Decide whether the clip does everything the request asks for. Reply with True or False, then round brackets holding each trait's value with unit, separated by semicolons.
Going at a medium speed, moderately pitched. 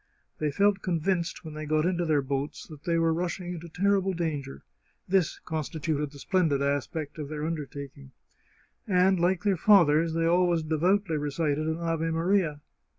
True (170 wpm; 165 Hz)